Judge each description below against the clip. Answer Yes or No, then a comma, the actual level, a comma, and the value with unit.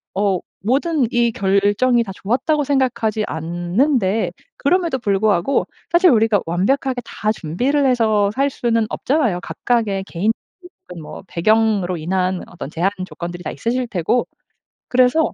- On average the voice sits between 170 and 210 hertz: No, high, 220 Hz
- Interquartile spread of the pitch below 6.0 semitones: Yes, average, 5.3 semitones